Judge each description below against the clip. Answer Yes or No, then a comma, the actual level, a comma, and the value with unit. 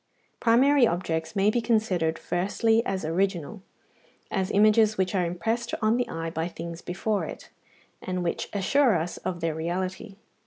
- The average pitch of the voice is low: No, high, 190 Hz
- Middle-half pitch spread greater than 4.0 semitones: Yes, average, 4.4 semitones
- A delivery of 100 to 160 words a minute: Yes, average, 155 wpm